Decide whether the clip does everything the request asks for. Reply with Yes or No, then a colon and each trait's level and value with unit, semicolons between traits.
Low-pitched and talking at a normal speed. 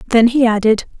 No: high, 230 Hz; average, 180 wpm